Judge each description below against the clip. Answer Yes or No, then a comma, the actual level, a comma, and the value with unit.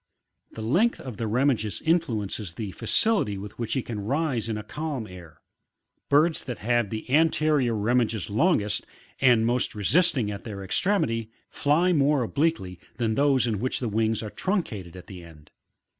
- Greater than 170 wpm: No, average, 165 wpm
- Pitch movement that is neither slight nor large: No, wide, 5.7 semitones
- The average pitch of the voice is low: Yes, low, 115 Hz